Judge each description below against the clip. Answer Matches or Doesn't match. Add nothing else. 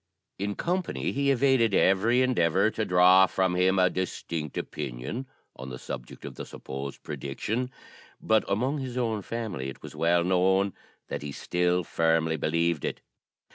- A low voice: Matches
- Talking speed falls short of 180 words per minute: Matches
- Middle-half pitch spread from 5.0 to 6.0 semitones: Matches